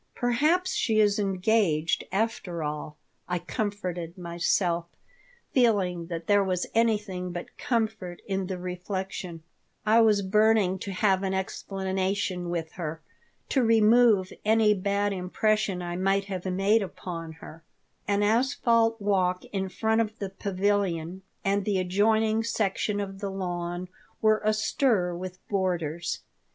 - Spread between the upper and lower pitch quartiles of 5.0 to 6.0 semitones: No, average, 3.1 semitones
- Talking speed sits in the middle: No, slow, 130 wpm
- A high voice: Yes, high, 195 Hz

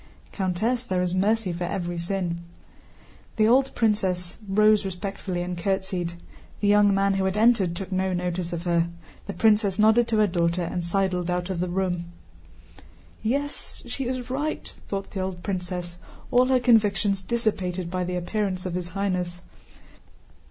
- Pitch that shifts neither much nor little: Yes, average, 3.1 semitones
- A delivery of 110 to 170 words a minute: Yes, average, 165 wpm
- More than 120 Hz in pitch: Yes, high, 190 Hz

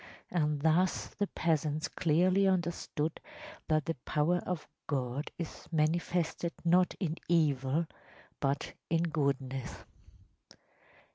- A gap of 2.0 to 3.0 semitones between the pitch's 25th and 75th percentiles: Yes, average, 2.7 semitones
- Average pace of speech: No, slow, 100 wpm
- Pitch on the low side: No, medium, 160 Hz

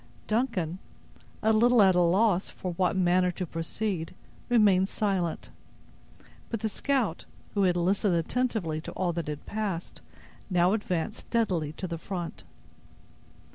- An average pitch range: Yes, average, 3.9 semitones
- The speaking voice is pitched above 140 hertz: Yes, medium, 185 Hz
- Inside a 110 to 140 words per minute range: Yes, slow, 135 wpm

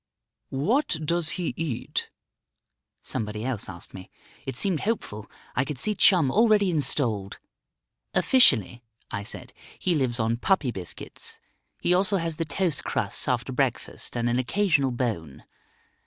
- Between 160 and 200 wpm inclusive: No, average, 140 wpm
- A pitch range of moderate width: No, wide, 7.5 semitones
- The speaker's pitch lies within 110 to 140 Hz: Yes, low, 135 Hz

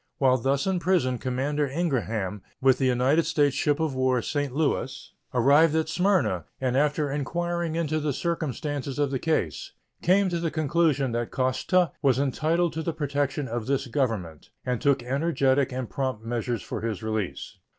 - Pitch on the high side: No, medium, 140 Hz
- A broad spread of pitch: No, average, 3.8 semitones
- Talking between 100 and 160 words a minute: No, average, 170 wpm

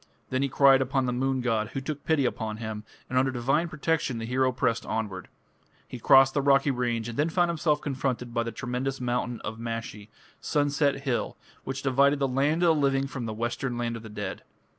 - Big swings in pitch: No, average, 2.9 semitones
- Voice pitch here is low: Yes, low, 130 Hz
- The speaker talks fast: Yes, fast, 210 wpm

